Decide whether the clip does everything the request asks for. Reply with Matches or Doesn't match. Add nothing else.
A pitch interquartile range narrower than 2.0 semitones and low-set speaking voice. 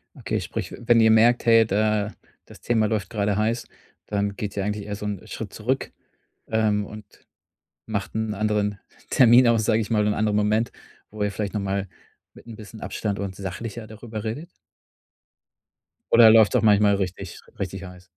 Matches